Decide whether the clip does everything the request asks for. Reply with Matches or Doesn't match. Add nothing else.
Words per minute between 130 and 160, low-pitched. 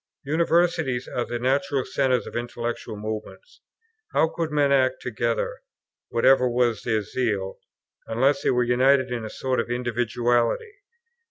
Matches